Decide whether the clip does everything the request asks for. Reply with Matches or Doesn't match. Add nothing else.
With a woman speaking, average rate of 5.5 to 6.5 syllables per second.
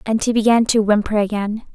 Matches